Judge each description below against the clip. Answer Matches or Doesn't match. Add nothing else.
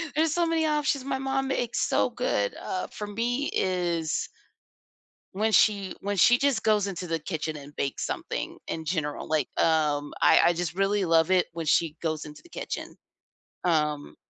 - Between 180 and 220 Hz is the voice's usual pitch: Matches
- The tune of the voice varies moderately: Doesn't match